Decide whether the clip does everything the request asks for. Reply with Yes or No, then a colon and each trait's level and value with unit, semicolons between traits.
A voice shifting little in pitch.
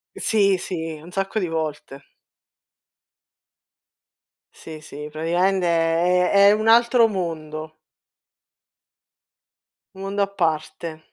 No: average, 3.8 semitones